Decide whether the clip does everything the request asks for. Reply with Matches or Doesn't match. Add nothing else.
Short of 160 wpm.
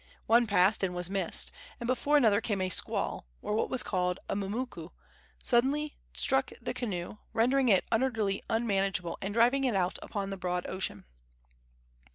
Doesn't match